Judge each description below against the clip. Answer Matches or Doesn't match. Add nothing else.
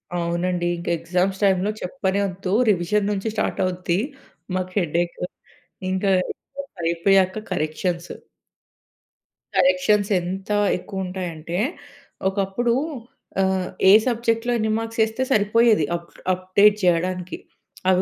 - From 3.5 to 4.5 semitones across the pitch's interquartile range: Doesn't match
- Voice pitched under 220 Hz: Matches